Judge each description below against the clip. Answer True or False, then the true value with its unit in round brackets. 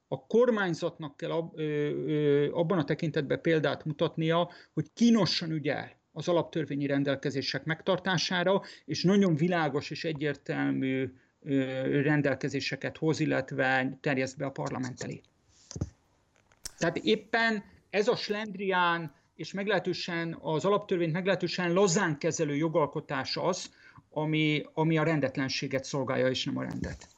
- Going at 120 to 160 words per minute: False (110 wpm)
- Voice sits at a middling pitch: True (155 Hz)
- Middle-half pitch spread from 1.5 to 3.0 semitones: False (3.6 semitones)